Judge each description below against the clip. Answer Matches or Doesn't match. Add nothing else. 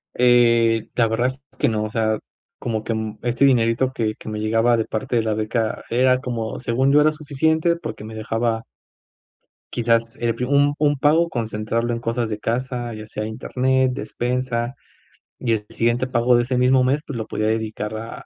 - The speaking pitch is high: Doesn't match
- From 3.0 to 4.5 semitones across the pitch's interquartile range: Doesn't match